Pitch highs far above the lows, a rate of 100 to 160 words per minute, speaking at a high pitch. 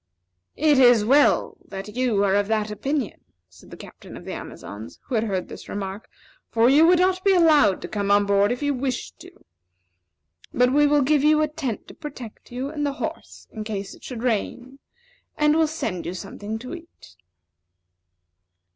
No: wide, 6.3 semitones; average, 190 wpm; high, 245 Hz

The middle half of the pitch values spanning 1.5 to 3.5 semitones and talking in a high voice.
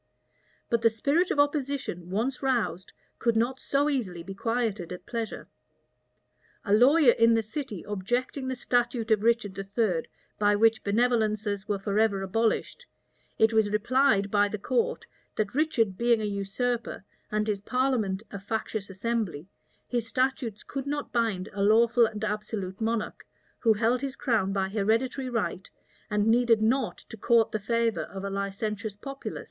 Yes: average, 3.2 semitones; high, 225 Hz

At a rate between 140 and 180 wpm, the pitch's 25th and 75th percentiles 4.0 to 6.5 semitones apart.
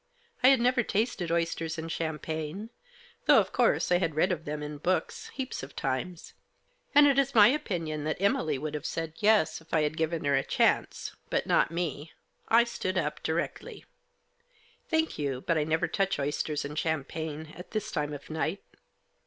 No: average, 195 wpm; average, 4.6 semitones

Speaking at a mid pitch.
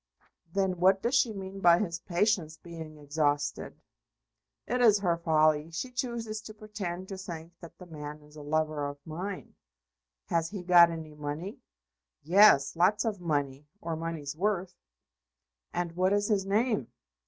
Yes: medium, 175 Hz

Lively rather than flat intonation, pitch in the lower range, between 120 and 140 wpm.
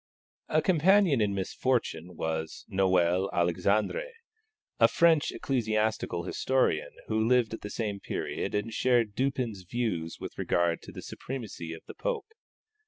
Yes: wide, 6.2 semitones; low, 110 Hz; slow, 135 wpm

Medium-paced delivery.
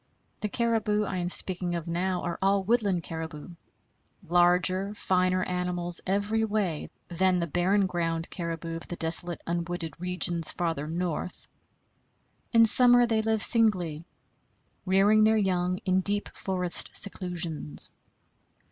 No: slow, 130 wpm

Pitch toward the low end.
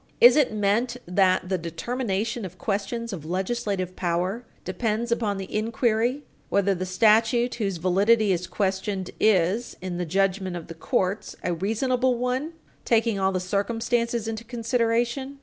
No: high, 210 Hz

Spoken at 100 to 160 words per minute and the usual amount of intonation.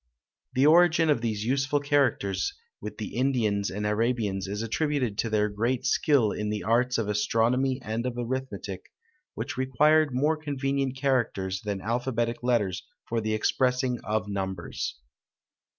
Yes: average, 145 wpm; average, 4.1 semitones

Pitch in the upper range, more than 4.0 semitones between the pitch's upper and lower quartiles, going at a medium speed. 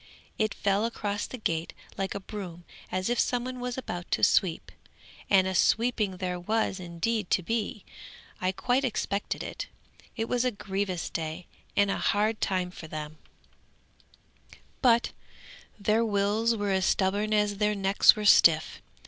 No: high, 200 Hz; average, 3.2 semitones; average, 155 wpm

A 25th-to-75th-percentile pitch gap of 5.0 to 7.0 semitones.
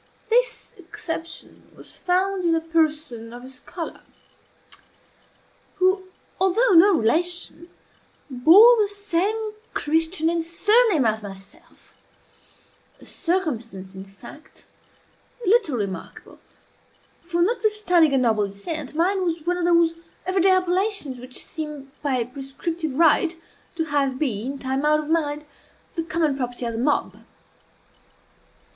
Yes: wide, 5.5 semitones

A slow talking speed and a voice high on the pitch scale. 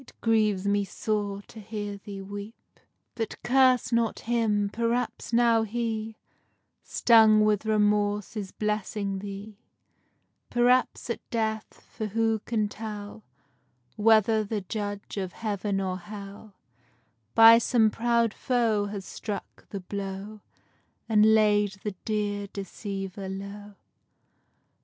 Yes: slow, 100 wpm; high, 210 Hz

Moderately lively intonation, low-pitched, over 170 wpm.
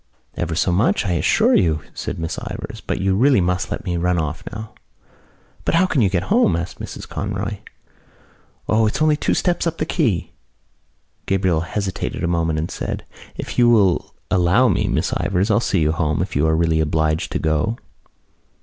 Yes: average, 4.7 semitones; very low, 90 Hz; average, 190 wpm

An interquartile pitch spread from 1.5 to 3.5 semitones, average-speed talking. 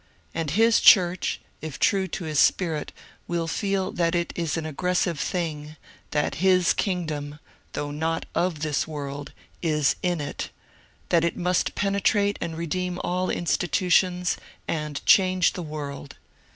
Yes: average, 3.1 semitones; average, 145 wpm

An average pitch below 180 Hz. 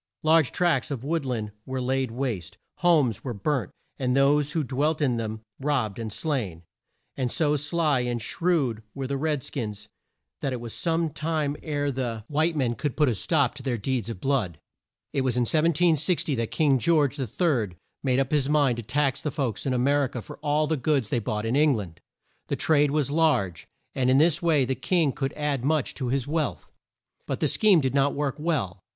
Yes: low, 135 Hz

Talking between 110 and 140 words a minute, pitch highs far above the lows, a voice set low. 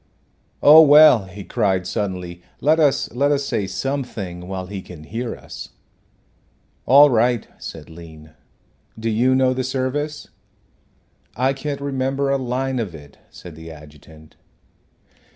Yes: slow, 135 wpm; wide, 7.2 semitones; low, 120 Hz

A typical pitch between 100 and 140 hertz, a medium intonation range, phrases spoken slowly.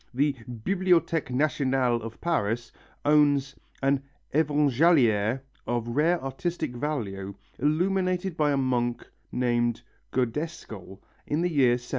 Yes: low, 135 Hz; average, 4.5 semitones; slow, 110 wpm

